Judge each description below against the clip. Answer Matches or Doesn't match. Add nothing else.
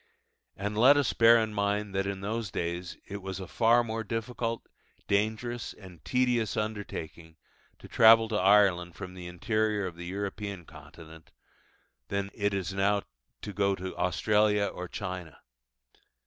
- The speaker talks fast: Doesn't match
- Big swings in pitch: Doesn't match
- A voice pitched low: Matches